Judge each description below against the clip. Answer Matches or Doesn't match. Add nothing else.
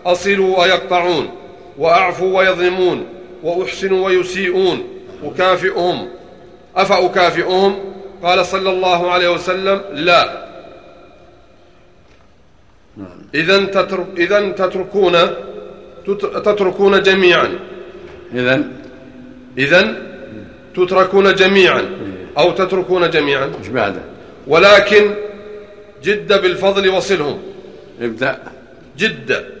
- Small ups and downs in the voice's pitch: Matches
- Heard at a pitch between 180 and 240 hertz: Matches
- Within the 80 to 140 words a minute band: Doesn't match